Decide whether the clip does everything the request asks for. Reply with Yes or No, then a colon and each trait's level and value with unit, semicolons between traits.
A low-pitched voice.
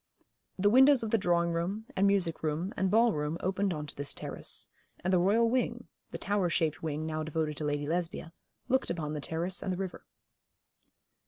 No: medium, 175 Hz